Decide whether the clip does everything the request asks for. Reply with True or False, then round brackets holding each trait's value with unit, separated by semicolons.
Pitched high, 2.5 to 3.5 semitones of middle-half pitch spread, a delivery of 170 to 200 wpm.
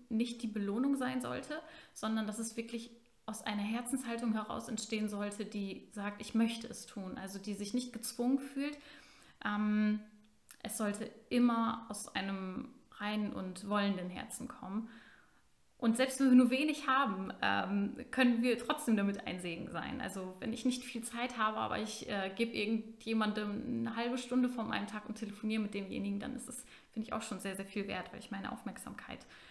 True (225 Hz; 3.0 semitones; 185 wpm)